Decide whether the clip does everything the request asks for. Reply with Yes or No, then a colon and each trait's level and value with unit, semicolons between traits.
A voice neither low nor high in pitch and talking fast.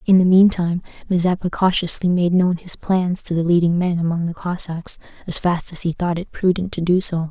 Yes: medium, 175 Hz; fast, 220 wpm